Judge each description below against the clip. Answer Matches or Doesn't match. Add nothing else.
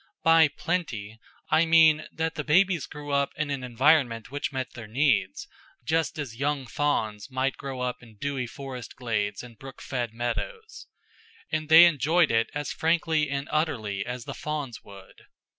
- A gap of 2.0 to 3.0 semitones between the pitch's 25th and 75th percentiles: Doesn't match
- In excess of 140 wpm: Matches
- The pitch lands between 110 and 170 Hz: Matches